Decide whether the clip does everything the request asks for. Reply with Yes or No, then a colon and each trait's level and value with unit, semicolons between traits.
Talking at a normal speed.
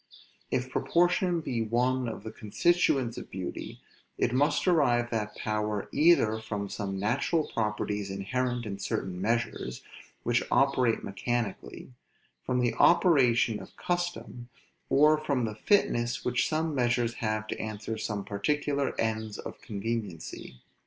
No: slow, 130 wpm